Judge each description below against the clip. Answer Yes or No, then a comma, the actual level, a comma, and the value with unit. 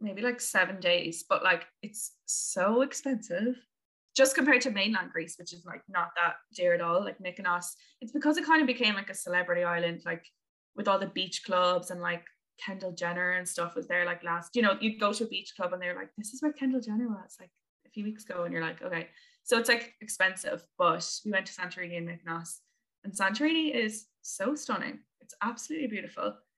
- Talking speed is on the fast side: Yes, fast, 215 wpm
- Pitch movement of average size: No, wide, 5.7 semitones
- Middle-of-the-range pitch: No, high, 195 Hz